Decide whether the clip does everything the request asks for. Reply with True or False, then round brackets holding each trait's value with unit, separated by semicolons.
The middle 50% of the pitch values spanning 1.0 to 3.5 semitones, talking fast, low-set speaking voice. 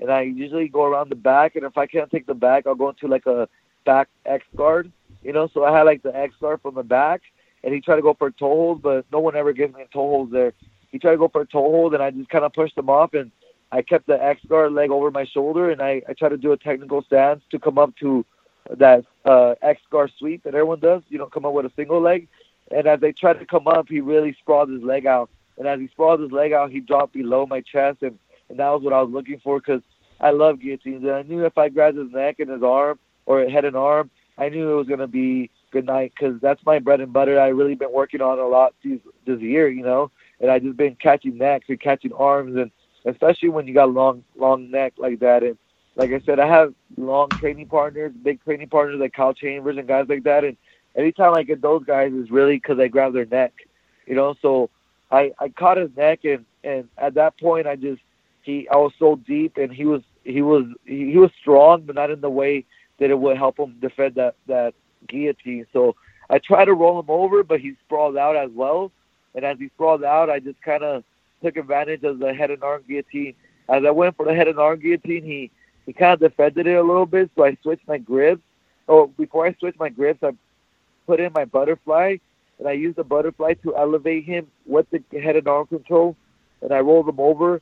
False (2.7 semitones; 250 wpm; 145 Hz)